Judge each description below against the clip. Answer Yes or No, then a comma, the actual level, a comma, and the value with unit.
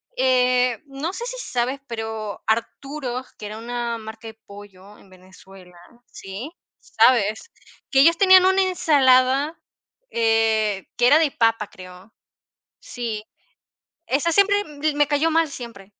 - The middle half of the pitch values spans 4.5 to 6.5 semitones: Yes, average, 5.2 semitones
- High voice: Yes, high, 245 Hz